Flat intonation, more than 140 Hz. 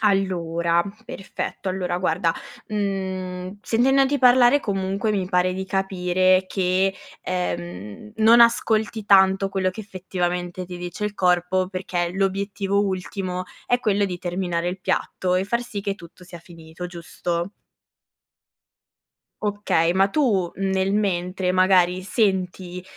Yes: narrow, 1.9 semitones; medium, 185 Hz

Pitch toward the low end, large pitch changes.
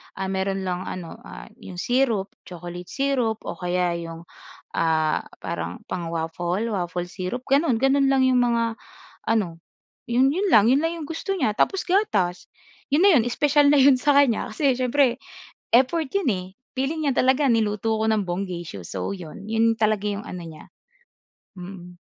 No: high, 220 Hz; wide, 7.0 semitones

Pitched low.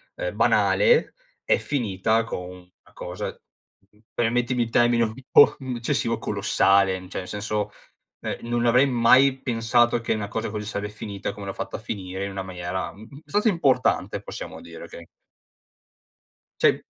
Yes: low, 115 Hz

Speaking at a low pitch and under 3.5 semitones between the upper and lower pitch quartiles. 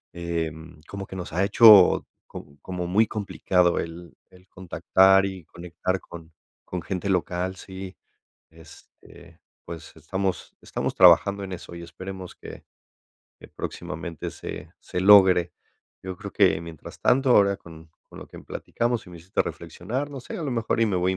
Yes: very low, 90 Hz; narrow, 2.5 semitones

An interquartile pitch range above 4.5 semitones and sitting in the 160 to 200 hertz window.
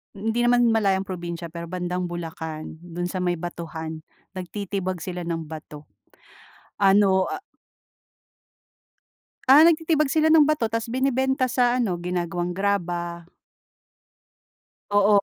Yes: average, 5.0 semitones; medium, 185 Hz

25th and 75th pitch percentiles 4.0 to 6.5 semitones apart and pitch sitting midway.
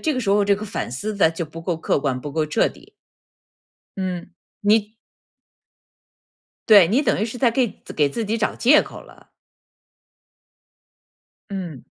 No: wide, 5.5 semitones; high, 200 Hz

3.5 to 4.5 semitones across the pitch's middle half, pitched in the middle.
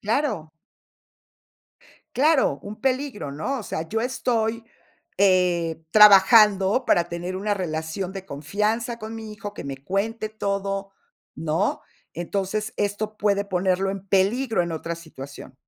No: average, 3.8 semitones; high, 200 Hz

